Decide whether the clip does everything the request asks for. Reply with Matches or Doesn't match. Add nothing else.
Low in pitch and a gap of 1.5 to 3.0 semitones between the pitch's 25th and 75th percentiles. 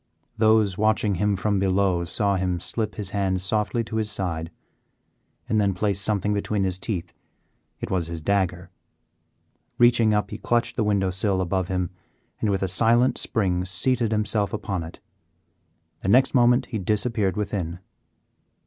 Matches